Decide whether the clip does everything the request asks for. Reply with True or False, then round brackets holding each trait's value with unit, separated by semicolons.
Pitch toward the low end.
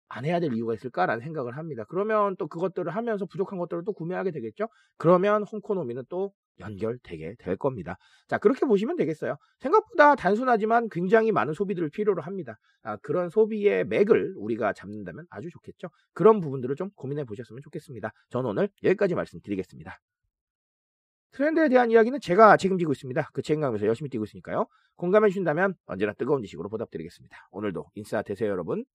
False (185 Hz)